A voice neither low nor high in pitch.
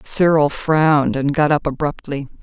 Yes: medium, 150 Hz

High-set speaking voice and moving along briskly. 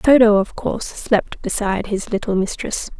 No: high, 210 Hz; average, 160 wpm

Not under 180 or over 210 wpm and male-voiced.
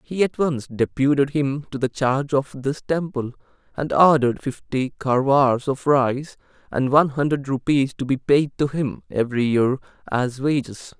No: average, 165 wpm; male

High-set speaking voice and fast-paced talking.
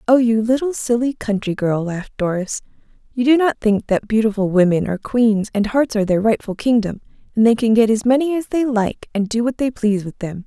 Yes: high, 225 Hz; fast, 225 wpm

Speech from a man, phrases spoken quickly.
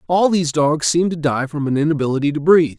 Yes: male; fast, 215 wpm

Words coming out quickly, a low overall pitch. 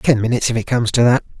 Yes: fast, 300 wpm; low, 115 Hz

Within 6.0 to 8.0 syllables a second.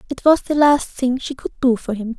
No: 5.3 syllables/s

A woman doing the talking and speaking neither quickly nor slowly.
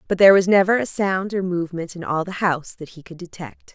No: female; fast, 255 wpm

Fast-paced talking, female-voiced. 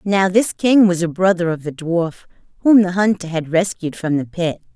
Yes: fast, 215 wpm; female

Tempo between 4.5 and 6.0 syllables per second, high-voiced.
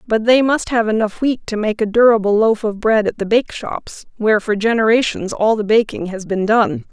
Yes: 5.3 syllables/s; high, 220 Hz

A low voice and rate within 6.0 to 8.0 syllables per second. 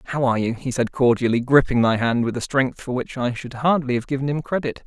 Yes: low, 130 Hz; 6.1 syllables/s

